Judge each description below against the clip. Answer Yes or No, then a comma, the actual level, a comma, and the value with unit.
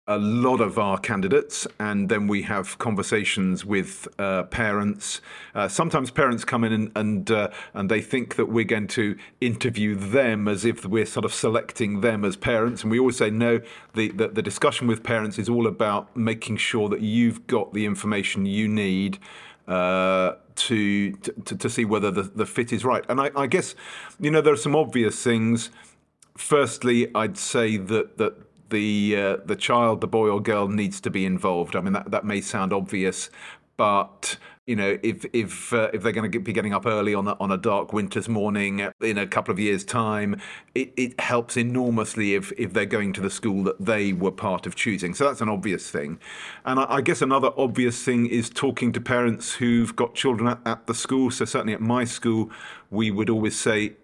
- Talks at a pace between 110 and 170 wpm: No, fast, 205 wpm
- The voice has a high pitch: No, low, 110 Hz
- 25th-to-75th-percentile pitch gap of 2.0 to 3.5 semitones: Yes, average, 2.7 semitones